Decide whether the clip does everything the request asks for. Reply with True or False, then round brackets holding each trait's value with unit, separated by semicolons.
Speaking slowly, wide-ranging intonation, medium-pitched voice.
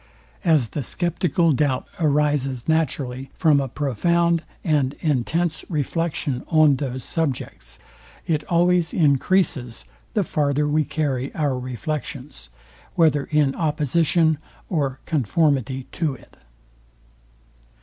False (105 wpm; 3.4 semitones; 150 Hz)